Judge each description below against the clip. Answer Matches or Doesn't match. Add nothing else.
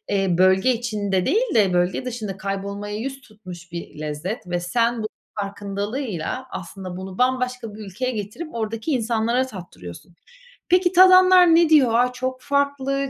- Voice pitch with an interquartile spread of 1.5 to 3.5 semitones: Doesn't match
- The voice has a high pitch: Matches